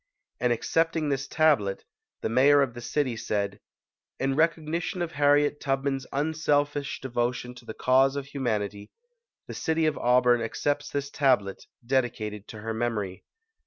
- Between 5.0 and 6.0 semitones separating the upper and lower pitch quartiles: No, average, 3.7 semitones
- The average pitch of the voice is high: No, low, 135 Hz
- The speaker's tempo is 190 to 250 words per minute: No, average, 150 wpm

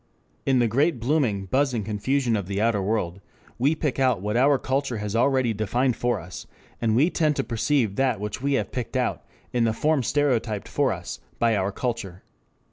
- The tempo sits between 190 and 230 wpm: Yes, average, 195 wpm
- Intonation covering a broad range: No, average, 4.3 semitones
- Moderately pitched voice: No, low, 120 Hz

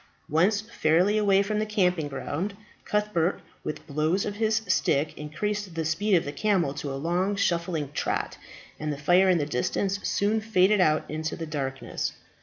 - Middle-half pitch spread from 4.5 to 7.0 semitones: Yes, average, 5.0 semitones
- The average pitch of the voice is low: No, medium, 180 Hz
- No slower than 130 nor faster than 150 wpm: No, average, 175 wpm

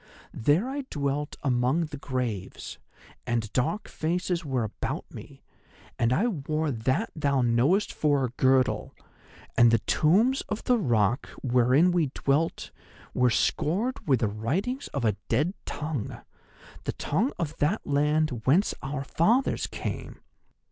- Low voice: No, medium, 145 Hz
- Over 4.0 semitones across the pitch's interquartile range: Yes, wide, 5.5 semitones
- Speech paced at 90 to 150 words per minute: Yes, slow, 135 wpm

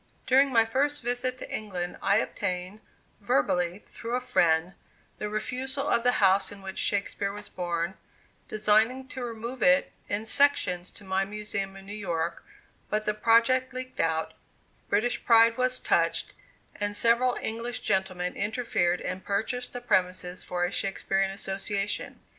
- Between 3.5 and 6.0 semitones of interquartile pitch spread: Yes, average, 4.3 semitones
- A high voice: Yes, high, 210 Hz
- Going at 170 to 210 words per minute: No, average, 150 wpm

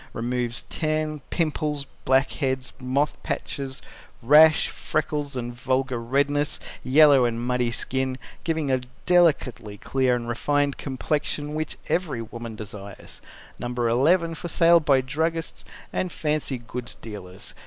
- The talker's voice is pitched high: No, low, 135 Hz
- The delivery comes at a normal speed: No, slow, 120 wpm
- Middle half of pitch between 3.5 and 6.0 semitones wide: Yes, average, 3.9 semitones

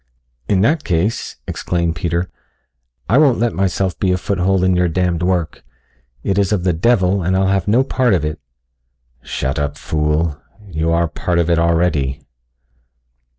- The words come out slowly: No, average, 170 wpm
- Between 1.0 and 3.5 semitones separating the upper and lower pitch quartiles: Yes, average, 2.7 semitones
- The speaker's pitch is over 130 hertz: No, very low, 90 Hz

